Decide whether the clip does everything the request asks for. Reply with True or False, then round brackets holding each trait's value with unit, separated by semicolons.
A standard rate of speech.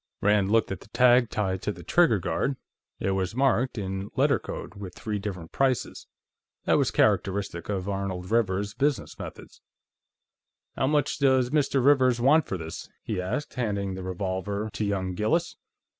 True (165 wpm)